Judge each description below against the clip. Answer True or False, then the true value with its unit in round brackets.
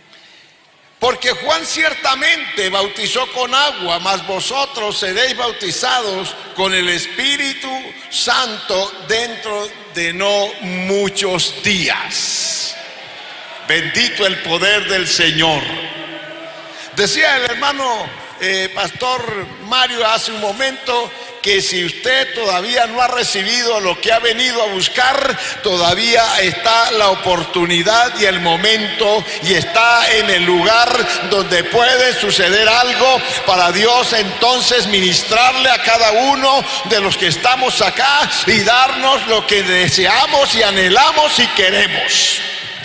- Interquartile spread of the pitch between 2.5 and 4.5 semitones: False (4.9 semitones)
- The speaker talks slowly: True (115 wpm)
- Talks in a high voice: True (225 Hz)